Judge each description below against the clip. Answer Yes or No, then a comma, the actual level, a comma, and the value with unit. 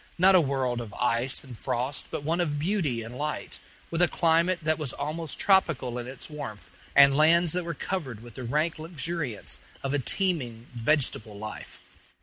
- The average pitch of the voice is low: No, medium, 145 Hz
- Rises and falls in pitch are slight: No, average, 5.3 semitones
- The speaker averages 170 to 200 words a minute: Yes, average, 180 wpm